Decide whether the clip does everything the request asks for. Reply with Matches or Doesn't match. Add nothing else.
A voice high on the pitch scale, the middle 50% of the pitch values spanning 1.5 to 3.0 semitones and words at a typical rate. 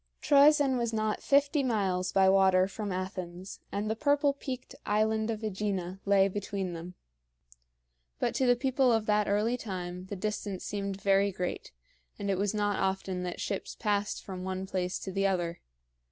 Matches